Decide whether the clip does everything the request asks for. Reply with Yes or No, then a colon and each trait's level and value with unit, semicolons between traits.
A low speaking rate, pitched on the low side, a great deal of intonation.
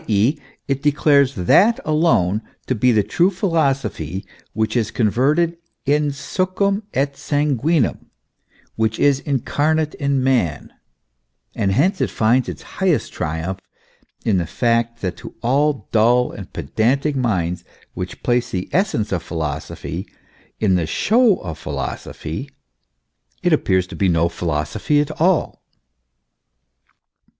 Yes: slow, 125 wpm; low, 125 Hz; wide, 7.5 semitones